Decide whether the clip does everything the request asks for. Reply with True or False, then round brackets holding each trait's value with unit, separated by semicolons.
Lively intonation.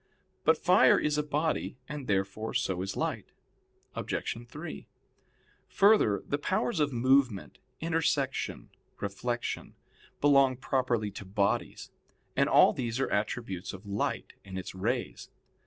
True (6.1 semitones)